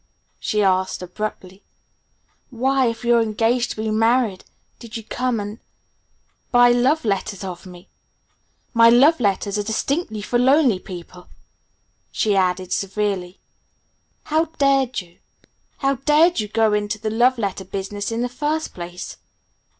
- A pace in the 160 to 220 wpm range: No, average, 140 wpm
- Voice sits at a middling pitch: No, high, 220 Hz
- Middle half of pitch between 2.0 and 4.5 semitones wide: Yes, average, 4.1 semitones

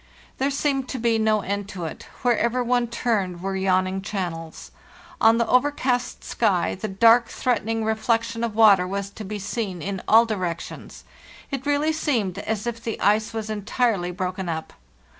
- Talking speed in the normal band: Yes, average, 165 wpm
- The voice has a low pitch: No, high, 220 Hz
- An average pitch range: Yes, average, 3.6 semitones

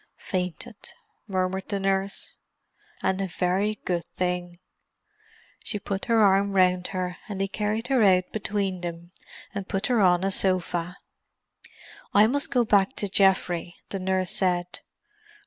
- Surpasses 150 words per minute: No, average, 145 wpm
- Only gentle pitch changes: Yes, narrow, 1.9 semitones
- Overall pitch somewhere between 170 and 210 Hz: Yes, high, 190 Hz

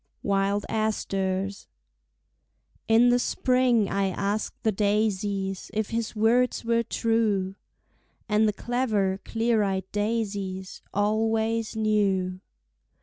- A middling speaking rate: No, slow, 100 wpm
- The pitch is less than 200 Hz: No, high, 210 Hz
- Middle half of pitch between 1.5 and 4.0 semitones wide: Yes, narrow, 2.4 semitones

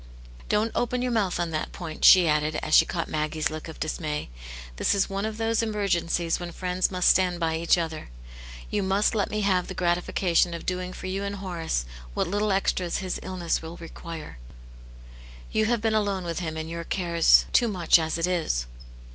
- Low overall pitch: No, medium, 180 Hz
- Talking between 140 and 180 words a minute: No, average, 195 wpm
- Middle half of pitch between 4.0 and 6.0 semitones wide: No, average, 3.2 semitones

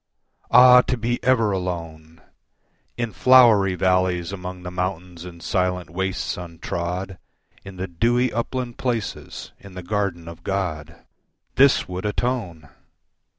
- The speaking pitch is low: Yes, very low, 95 Hz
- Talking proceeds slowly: Yes, slow, 125 wpm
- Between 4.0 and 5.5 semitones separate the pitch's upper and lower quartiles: Yes, average, 4.6 semitones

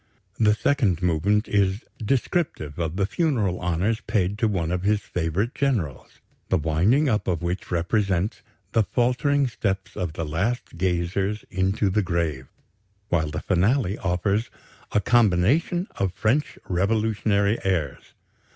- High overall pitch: No, low, 100 Hz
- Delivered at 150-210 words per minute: No, slow, 135 wpm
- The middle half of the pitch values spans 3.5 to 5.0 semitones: Yes, average, 4.1 semitones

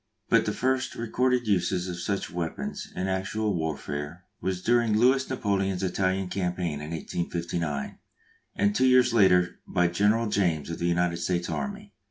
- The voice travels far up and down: No, average, 4.0 semitones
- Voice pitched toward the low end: Yes, very low, 95 Hz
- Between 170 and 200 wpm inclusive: No, average, 155 wpm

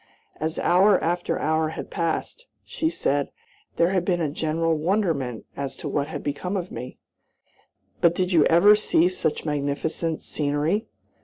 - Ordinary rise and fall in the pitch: Yes, average, 3.4 semitones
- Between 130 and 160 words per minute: Yes, average, 155 wpm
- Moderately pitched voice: Yes, medium, 165 Hz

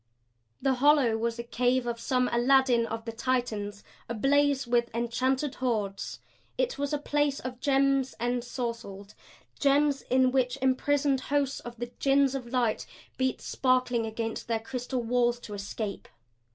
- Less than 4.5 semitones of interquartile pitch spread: Yes, narrow, 2.6 semitones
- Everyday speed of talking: Yes, average, 145 wpm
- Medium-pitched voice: No, very high, 250 Hz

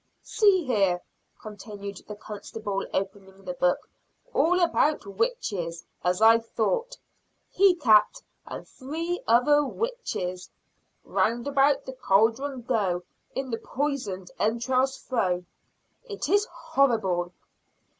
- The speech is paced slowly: Yes, slow, 110 wpm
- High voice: Yes, high, 230 Hz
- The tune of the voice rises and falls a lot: Yes, wide, 6.8 semitones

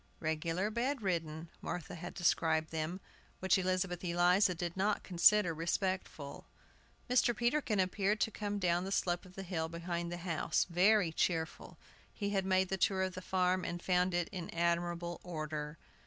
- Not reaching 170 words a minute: Yes, average, 160 wpm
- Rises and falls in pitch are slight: Yes, narrow, 2.1 semitones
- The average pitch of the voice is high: No, medium, 180 Hz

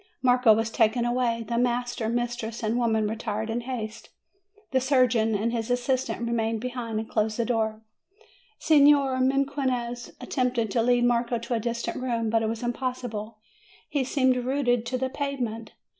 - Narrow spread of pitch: Yes, narrow, 2.0 semitones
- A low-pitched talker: No, high, 240 Hz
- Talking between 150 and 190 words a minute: Yes, average, 165 wpm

